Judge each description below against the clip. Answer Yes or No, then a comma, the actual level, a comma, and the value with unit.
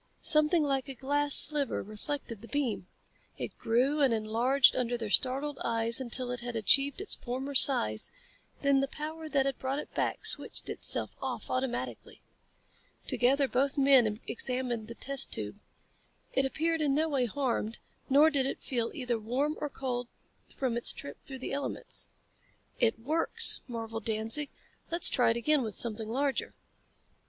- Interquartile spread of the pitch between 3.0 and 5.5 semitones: Yes, average, 3.4 semitones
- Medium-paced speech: Yes, average, 160 wpm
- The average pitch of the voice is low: No, very high, 265 Hz